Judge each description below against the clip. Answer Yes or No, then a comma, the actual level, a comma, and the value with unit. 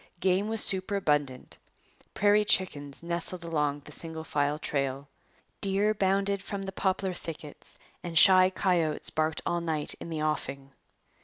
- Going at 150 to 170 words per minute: No, average, 140 wpm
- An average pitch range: Yes, average, 4.3 semitones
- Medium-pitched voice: Yes, medium, 170 Hz